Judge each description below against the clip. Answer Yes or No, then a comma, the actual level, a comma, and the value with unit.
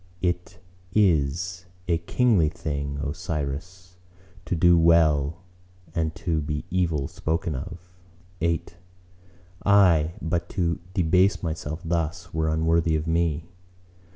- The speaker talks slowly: Yes, slow, 120 wpm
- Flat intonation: Yes, narrow, 2.3 semitones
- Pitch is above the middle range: No, very low, 85 Hz